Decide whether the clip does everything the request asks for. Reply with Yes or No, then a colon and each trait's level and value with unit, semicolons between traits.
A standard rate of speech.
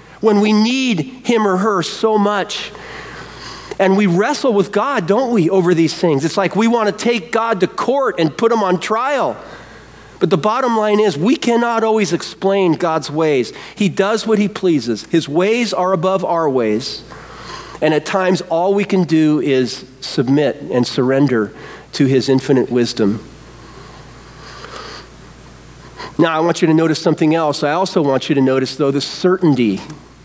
Yes: average, 170 wpm